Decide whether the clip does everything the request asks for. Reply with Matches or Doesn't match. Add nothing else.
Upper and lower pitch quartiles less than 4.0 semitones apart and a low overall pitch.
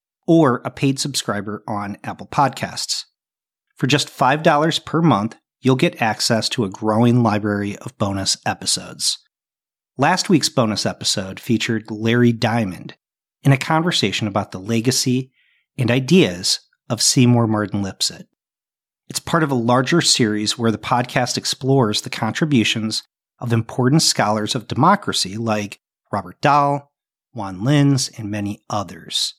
Doesn't match